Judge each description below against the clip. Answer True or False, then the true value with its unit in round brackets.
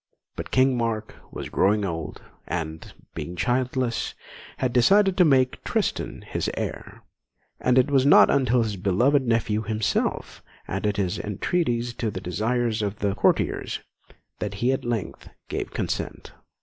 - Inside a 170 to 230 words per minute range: False (145 wpm)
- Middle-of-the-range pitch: False (115 Hz)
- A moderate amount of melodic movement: True (3.9 semitones)